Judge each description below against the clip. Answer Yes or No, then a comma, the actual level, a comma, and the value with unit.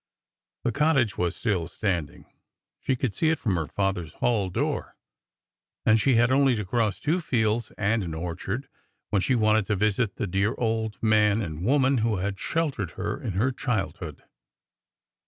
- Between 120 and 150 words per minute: No, average, 170 wpm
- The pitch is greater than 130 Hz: No, low, 110 Hz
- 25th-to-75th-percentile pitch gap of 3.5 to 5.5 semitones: Yes, average, 4.1 semitones